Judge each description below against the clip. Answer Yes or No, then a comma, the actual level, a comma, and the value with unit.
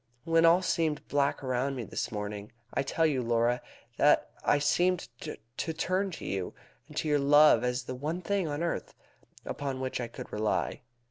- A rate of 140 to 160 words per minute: No, average, 185 wpm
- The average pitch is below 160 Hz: Yes, medium, 140 Hz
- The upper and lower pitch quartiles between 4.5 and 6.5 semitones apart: Yes, average, 4.9 semitones